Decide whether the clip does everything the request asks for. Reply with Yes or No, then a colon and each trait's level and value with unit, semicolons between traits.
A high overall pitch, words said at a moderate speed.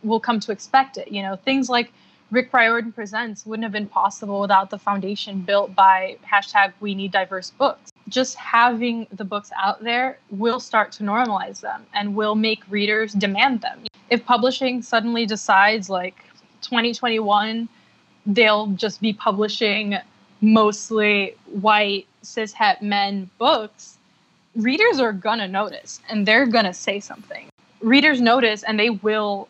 Yes: high, 215 Hz; average, 145 wpm